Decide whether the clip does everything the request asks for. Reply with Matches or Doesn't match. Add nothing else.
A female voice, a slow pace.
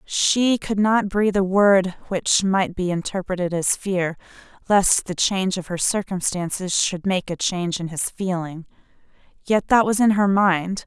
Doesn't match